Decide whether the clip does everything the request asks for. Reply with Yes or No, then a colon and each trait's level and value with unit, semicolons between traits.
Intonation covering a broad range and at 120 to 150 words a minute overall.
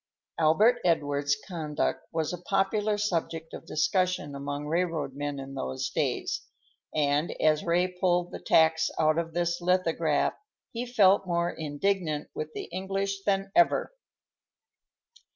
No: average, 3.7 semitones; slow, 135 wpm